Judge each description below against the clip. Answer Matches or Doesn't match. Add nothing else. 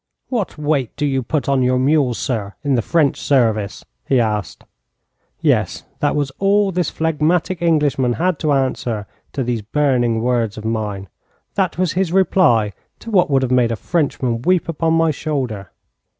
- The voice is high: Doesn't match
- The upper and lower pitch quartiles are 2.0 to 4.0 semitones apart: Doesn't match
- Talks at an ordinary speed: Matches